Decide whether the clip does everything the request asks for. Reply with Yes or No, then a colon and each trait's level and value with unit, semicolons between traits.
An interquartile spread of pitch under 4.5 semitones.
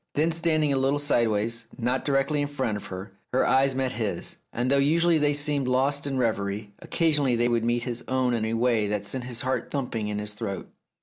Yes: average, 4.0 semitones